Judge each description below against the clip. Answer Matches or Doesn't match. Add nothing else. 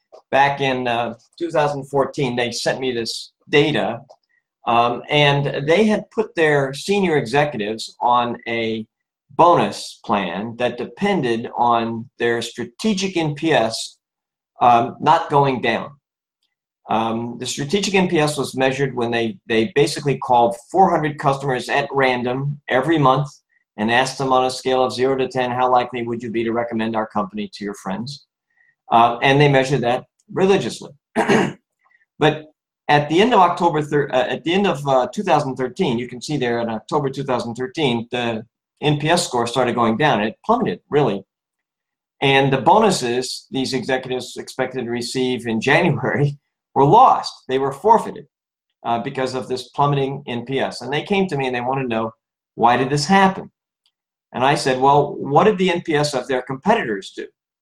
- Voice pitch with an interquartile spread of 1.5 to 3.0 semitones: Doesn't match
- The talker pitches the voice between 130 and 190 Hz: Matches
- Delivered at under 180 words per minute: Matches